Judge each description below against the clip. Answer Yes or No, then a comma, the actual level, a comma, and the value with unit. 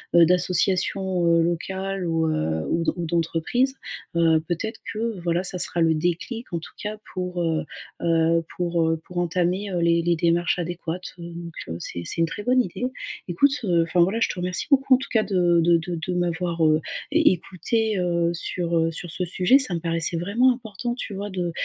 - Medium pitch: Yes, medium, 175 Hz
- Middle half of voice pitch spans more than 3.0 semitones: No, narrow, 2.5 semitones